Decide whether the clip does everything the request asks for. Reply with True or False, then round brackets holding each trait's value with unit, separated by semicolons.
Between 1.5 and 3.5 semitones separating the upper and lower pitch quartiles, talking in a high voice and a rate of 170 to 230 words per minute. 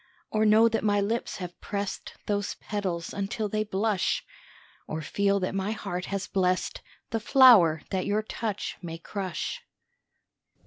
False (2.6 semitones; 200 Hz; 145 wpm)